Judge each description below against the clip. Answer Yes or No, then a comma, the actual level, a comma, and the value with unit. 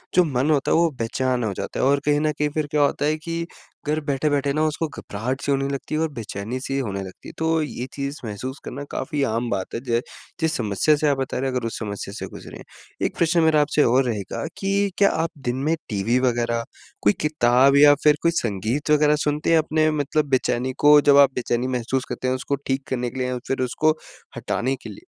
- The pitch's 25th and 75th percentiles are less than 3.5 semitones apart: No, average, 3.9 semitones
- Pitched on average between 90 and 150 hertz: Yes, low, 135 Hz